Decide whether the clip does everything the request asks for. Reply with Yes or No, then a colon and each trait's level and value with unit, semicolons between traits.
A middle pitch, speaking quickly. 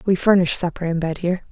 Yes: medium, 175 Hz; fast, 240 wpm